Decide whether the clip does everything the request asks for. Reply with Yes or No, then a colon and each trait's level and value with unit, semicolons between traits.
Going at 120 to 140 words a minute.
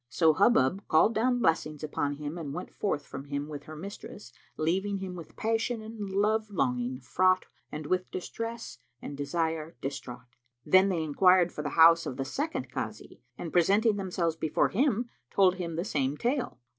No: average, 175 wpm